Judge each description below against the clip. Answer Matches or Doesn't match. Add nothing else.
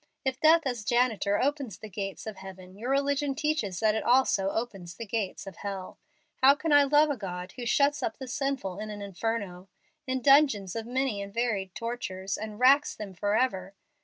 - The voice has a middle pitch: Doesn't match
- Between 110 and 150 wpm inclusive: Doesn't match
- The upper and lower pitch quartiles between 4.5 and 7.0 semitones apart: Matches